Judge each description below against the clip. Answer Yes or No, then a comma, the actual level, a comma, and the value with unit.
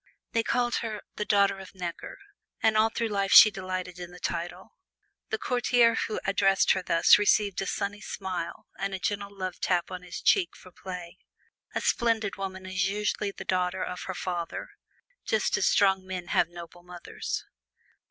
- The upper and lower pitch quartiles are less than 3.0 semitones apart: Yes, narrow, 2.4 semitones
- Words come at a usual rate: Yes, average, 175 wpm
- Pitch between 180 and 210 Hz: Yes, high, 190 Hz